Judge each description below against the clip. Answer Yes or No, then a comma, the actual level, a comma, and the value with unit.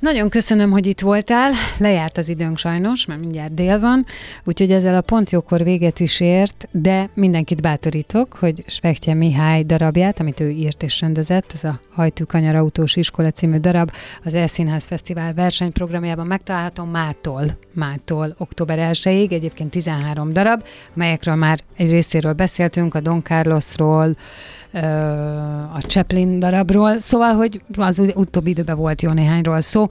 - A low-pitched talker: No, medium, 170 Hz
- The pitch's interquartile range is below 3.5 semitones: Yes, average, 2.9 semitones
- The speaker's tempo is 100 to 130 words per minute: No, average, 150 wpm